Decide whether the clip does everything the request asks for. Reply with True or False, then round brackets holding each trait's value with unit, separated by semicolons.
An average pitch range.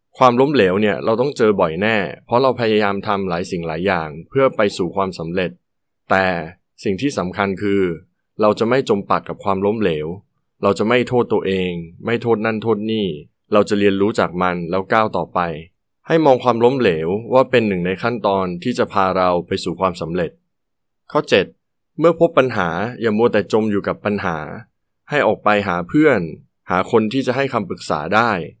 True (4.0 semitones)